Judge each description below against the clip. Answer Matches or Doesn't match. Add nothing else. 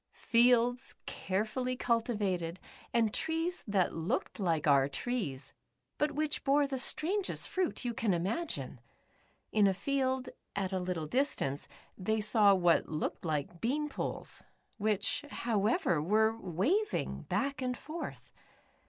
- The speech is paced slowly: Matches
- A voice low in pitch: Doesn't match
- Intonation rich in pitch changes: Matches